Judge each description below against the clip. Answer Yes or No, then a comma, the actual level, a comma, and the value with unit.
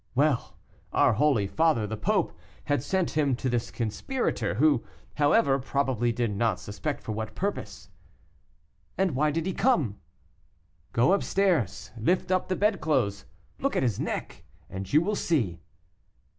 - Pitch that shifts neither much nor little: No, wide, 7.1 semitones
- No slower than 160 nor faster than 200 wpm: No, average, 150 wpm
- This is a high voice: No, low, 135 Hz